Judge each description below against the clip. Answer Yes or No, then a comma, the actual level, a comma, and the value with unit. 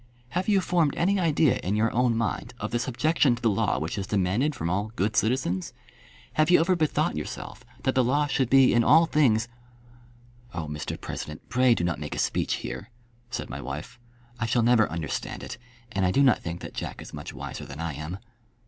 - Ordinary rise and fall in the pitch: No, wide, 6.5 semitones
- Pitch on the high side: No, low, 120 Hz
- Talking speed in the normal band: No, fast, 215 wpm